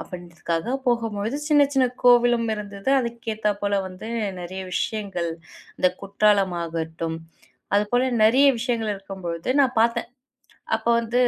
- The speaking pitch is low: No, high, 210 Hz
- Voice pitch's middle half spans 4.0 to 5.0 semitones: Yes, average, 4.3 semitones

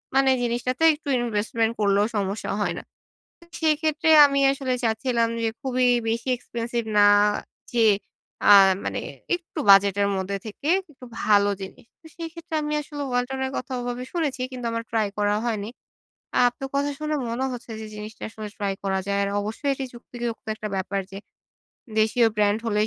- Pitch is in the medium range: No, high, 235 Hz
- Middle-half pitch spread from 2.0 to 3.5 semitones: No, average, 4.2 semitones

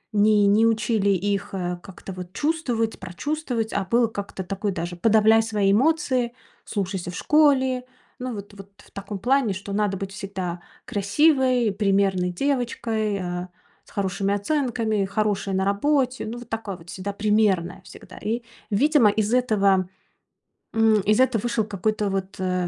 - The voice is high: Yes, high, 210 Hz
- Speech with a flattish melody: No, average, 3.3 semitones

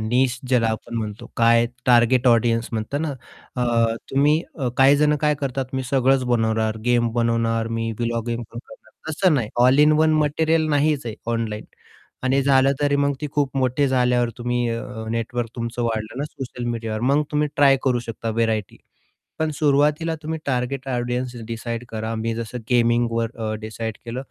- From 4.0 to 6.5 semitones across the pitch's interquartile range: No, average, 3.2 semitones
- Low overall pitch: Yes, low, 120 Hz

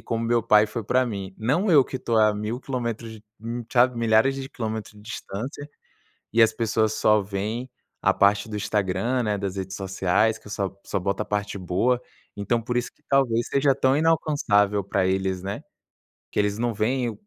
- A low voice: Yes, low, 110 Hz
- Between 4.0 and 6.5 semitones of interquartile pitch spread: No, average, 3.2 semitones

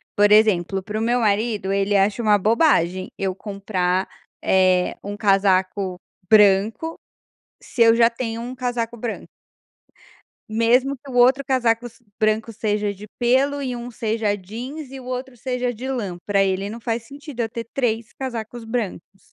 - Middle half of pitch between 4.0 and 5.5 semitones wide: No, average, 3.5 semitones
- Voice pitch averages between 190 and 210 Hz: No, high, 225 Hz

